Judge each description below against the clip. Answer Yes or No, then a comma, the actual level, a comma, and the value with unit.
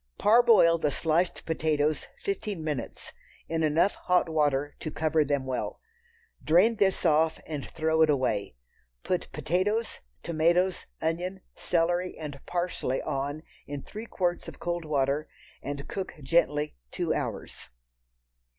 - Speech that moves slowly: Yes, slow, 130 wpm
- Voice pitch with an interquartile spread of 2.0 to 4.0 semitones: Yes, average, 3.4 semitones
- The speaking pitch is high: No, medium, 160 Hz